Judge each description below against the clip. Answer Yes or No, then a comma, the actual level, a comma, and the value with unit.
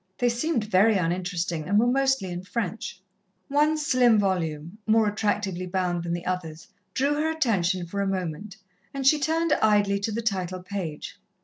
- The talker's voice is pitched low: No, high, 200 Hz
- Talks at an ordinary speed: Yes, average, 170 wpm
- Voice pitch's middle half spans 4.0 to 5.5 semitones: Yes, average, 5.0 semitones